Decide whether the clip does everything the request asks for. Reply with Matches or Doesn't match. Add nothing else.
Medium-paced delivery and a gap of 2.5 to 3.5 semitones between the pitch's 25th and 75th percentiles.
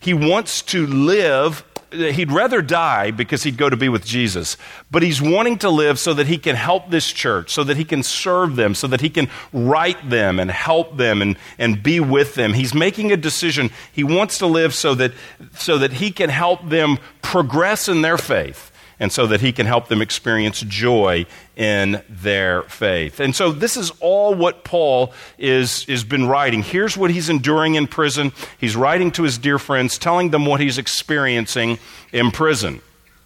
Doesn't match